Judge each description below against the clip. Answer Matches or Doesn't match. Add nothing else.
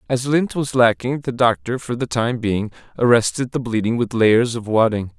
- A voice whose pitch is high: Doesn't match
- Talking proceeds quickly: Doesn't match